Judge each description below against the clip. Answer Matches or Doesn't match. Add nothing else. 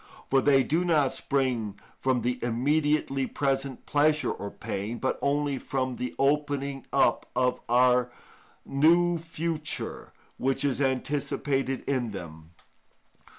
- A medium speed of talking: Doesn't match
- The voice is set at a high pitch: Doesn't match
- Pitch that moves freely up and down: Doesn't match